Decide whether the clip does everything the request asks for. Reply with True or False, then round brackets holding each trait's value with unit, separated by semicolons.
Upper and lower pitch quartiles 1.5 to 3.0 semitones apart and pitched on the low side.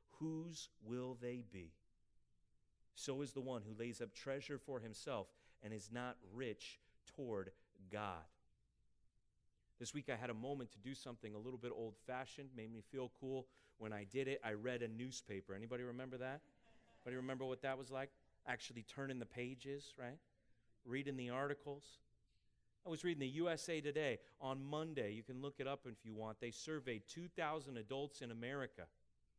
False (3.4 semitones; 125 Hz)